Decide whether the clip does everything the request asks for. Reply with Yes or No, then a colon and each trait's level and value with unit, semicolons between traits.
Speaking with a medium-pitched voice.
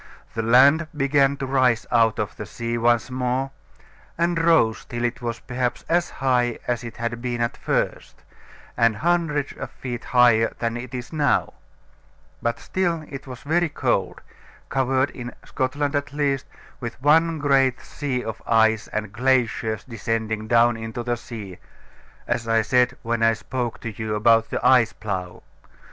No: low, 120 Hz